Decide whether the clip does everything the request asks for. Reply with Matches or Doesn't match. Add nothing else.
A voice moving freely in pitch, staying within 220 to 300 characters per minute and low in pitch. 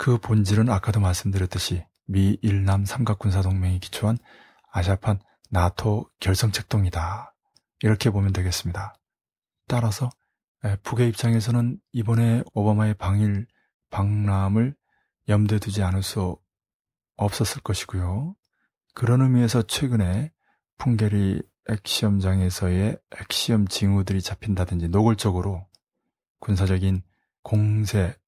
Doesn't match